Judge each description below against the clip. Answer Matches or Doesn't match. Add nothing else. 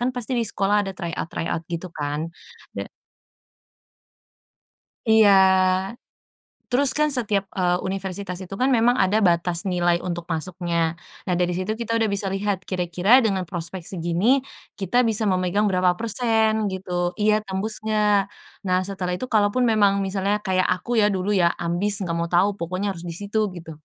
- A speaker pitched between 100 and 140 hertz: Doesn't match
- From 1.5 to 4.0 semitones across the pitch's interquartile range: Matches